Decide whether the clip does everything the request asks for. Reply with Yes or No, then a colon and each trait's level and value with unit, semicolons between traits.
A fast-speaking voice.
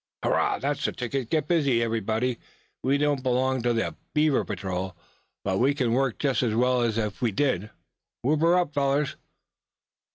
No: average, 170 wpm